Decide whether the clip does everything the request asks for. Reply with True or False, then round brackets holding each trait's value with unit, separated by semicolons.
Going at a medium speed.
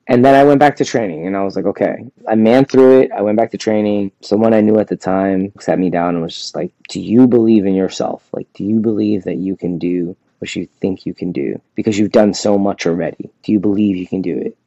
False (270 wpm)